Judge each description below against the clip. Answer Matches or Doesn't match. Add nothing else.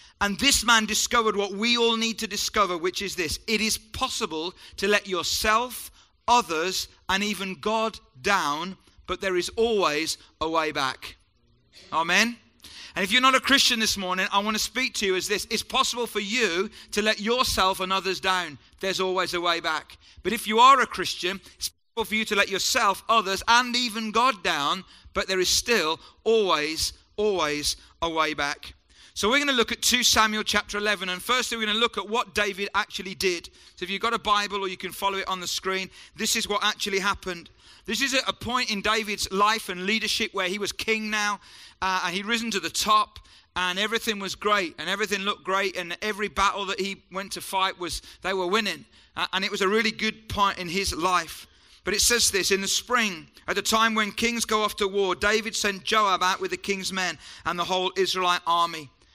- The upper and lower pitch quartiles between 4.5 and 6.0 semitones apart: Doesn't match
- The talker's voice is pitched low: Doesn't match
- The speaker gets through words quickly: Matches